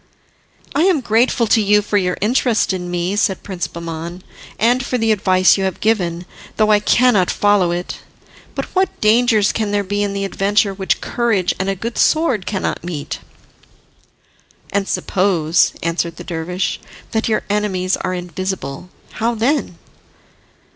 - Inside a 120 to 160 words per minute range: Yes, average, 155 wpm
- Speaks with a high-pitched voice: Yes, high, 200 Hz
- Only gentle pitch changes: No, average, 3.5 semitones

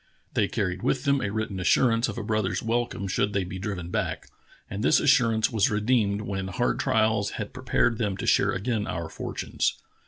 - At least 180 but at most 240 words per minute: Yes, average, 195 wpm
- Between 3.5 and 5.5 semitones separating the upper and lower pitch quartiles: No, average, 3.1 semitones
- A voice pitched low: Yes, low, 105 Hz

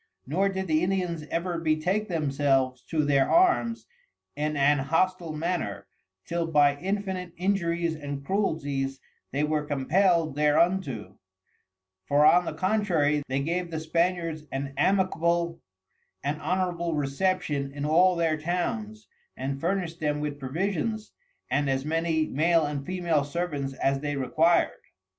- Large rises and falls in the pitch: No, average, 3.8 semitones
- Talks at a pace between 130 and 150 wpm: Yes, slow, 135 wpm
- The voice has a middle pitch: Yes, medium, 160 Hz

